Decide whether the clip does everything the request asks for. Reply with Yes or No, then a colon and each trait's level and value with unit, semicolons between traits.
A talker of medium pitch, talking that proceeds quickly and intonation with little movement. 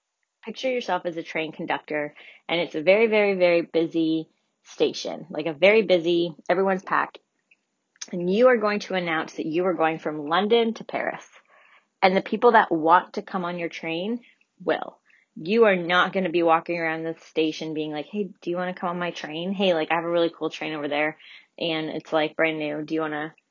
No: medium, 170 Hz; fast, 215 wpm; average, 3.2 semitones